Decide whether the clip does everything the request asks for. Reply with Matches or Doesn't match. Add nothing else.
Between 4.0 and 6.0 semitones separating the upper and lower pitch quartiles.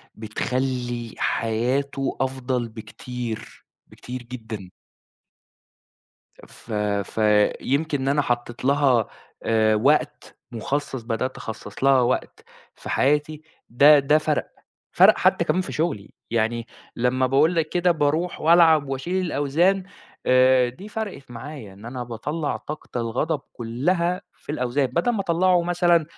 Matches